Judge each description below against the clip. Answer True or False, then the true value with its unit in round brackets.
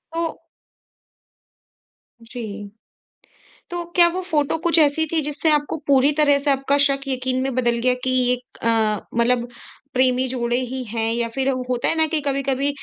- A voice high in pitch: True (265 Hz)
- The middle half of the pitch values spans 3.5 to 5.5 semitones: False (3.1 semitones)